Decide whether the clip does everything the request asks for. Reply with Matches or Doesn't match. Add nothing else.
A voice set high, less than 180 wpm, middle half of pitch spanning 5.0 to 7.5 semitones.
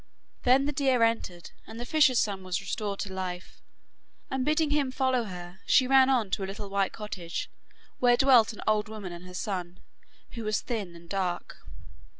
Doesn't match